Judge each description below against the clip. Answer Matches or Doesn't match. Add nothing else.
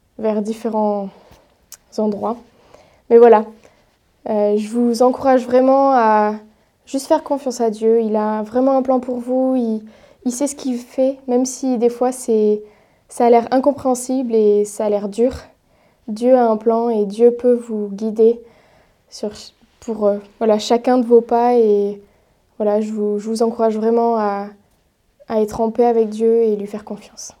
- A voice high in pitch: Matches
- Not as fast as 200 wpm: Matches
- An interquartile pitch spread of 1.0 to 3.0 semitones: Matches